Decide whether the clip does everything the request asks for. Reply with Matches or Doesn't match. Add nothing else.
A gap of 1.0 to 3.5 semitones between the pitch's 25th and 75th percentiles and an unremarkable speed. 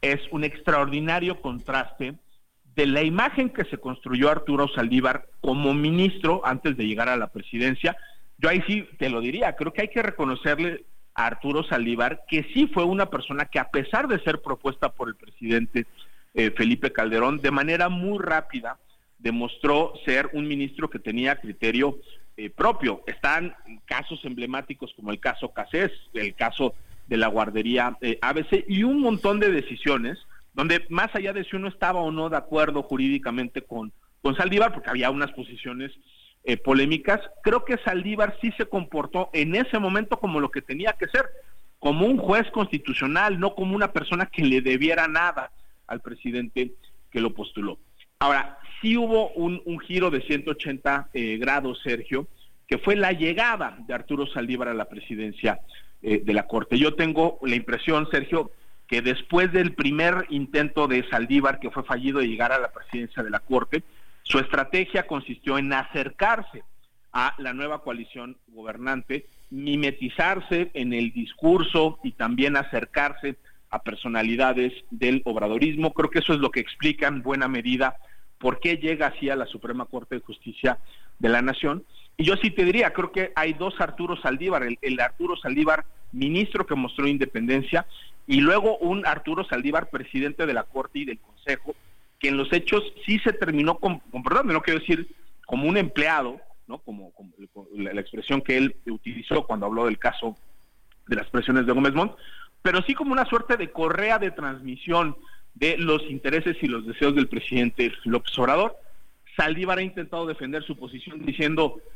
Doesn't match